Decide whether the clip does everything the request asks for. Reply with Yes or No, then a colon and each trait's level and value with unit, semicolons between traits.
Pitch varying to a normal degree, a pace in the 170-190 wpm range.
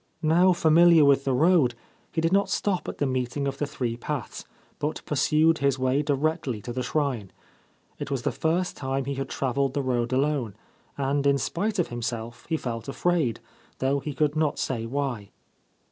Yes: average, 3.3 semitones; average, 185 wpm